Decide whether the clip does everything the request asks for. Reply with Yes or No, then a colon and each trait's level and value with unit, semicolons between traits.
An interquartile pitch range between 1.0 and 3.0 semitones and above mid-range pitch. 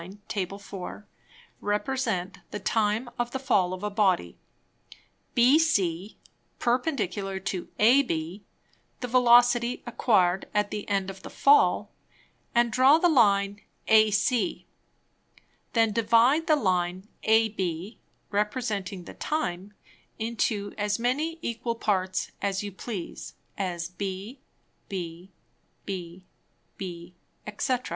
No: average, 4.1 semitones; high, 210 Hz